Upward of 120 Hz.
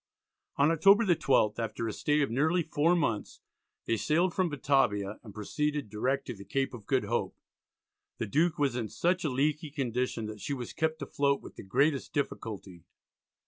Yes: medium, 140 Hz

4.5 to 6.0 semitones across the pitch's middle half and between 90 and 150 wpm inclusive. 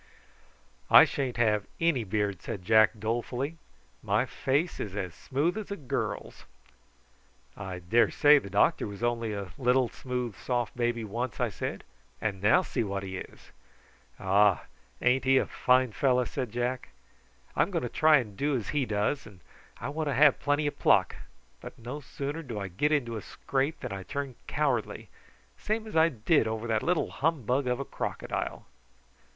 No: average, 4.9 semitones; average, 175 wpm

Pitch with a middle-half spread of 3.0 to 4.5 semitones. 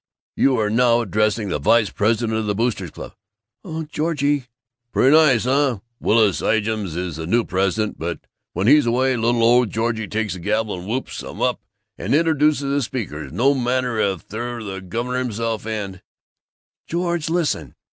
Yes: average, 3.8 semitones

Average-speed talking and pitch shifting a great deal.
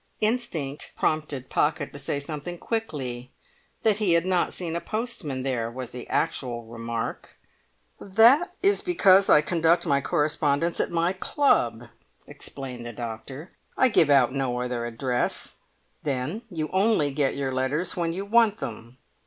Yes: average, 150 wpm; wide, 6.5 semitones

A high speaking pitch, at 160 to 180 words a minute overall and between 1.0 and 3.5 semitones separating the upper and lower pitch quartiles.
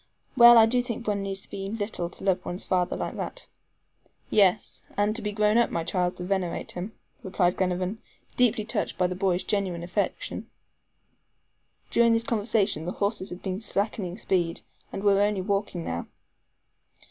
Yes: high, 195 Hz; average, 170 wpm; average, 2.9 semitones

